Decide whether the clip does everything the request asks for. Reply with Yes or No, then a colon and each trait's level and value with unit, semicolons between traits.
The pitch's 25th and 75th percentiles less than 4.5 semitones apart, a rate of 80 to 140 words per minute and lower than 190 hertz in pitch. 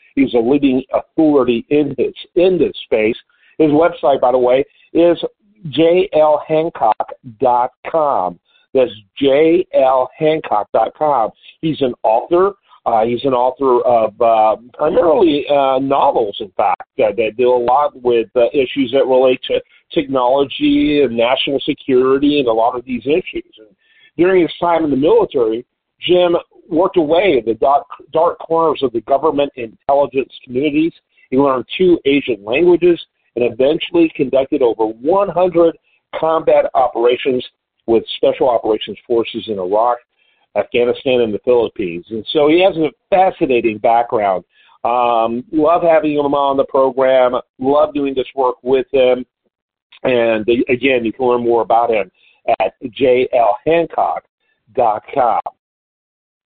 No: average, 5.2 semitones; slow, 135 wpm; medium, 140 Hz